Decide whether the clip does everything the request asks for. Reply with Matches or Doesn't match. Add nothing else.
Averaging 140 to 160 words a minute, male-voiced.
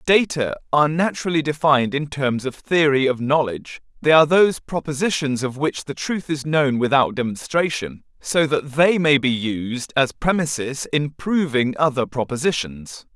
Matches